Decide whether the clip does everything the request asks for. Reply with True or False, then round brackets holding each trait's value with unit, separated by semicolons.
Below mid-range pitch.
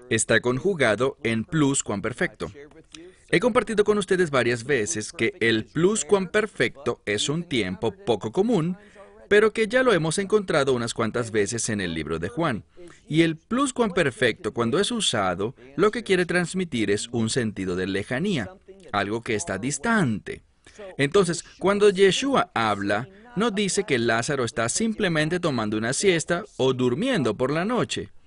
False (155 Hz)